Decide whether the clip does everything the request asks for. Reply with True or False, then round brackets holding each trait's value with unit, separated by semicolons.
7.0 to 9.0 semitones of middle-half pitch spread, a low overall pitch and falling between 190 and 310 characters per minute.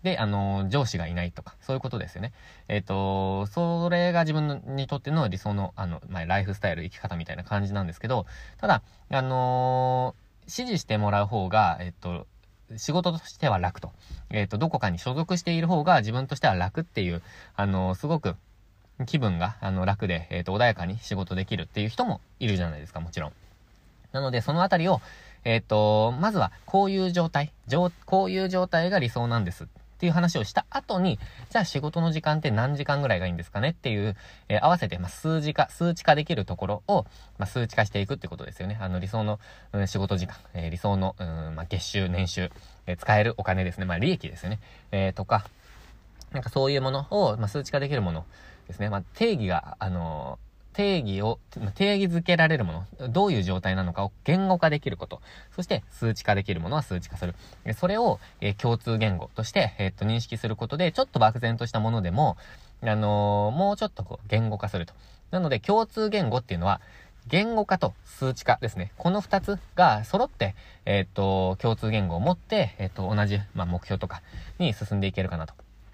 False (7.3 semitones; 105 Hz; 400 characters per minute)